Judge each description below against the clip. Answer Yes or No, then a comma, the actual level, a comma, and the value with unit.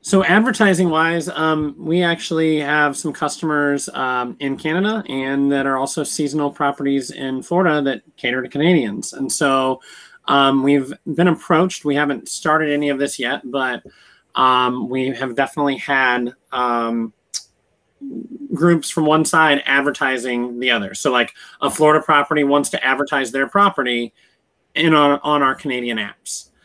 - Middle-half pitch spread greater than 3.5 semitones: No, average, 3.1 semitones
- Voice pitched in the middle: Yes, medium, 145 Hz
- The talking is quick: No, average, 150 wpm